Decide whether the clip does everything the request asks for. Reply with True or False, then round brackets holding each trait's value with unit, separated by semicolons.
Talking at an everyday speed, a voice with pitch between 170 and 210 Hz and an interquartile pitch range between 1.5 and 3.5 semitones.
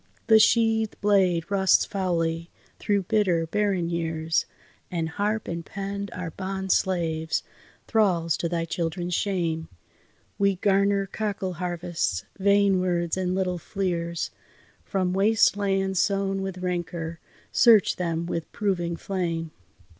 False (125 wpm; 185 Hz; 2.8 semitones)